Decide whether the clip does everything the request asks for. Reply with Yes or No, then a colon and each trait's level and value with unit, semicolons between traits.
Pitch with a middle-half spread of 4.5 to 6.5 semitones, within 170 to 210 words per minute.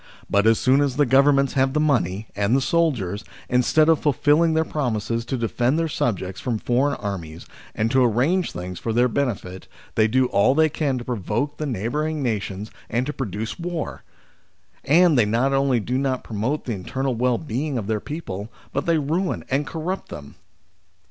Yes: average, 5.1 semitones; average, 185 wpm